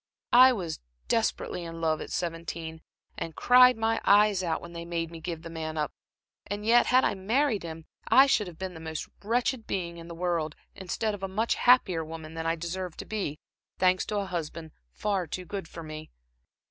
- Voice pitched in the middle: Yes, medium, 175 Hz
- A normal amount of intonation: Yes, average, 4.2 semitones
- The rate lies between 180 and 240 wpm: Yes, fast, 205 wpm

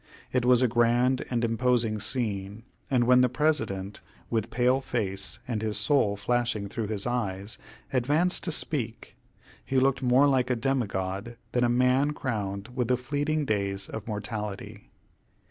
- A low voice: Yes, low, 120 Hz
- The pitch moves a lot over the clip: No, average, 3.5 semitones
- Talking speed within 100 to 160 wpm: Yes, average, 155 wpm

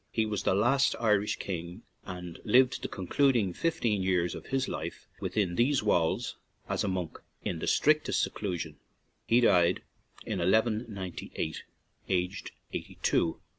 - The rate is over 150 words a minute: No, average, 145 wpm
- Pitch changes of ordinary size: Yes, average, 4.8 semitones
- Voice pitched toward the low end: Yes, low, 100 Hz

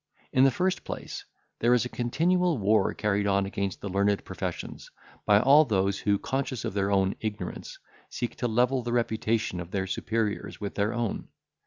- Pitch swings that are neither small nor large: Yes, average, 3.8 semitones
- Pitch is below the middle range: Yes, low, 110 Hz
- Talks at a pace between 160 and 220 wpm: Yes, average, 180 wpm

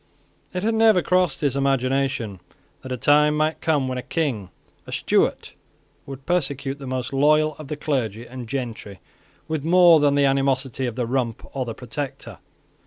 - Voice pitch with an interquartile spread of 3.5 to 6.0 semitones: No, average, 3.1 semitones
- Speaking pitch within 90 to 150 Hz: Yes, low, 135 Hz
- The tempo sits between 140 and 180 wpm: Yes, average, 175 wpm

